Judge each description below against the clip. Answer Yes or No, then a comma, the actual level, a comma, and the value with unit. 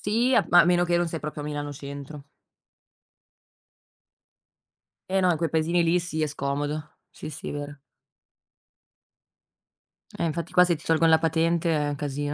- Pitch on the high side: No, medium, 160 Hz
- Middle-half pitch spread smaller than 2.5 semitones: No, average, 2.8 semitones